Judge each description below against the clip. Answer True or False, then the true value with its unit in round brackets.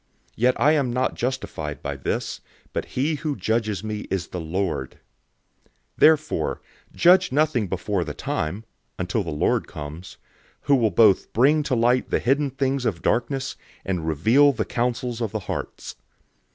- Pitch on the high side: False (120 Hz)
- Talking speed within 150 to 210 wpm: True (160 wpm)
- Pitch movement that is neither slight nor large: False (6.3 semitones)